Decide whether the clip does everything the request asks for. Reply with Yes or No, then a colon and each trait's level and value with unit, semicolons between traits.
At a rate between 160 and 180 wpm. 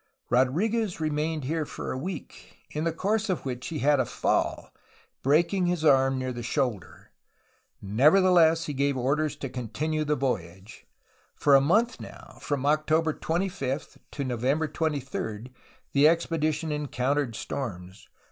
No: average, 140 wpm